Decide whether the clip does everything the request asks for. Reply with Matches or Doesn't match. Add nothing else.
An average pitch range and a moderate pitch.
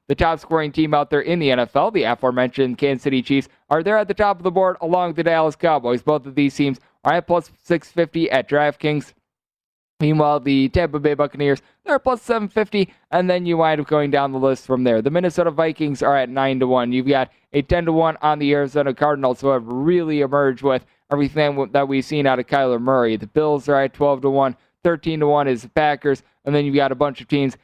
Matches